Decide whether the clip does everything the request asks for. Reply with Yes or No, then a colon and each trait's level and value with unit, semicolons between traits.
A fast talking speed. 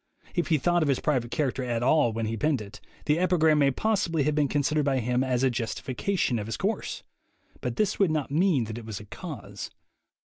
Yes: fast, 220 wpm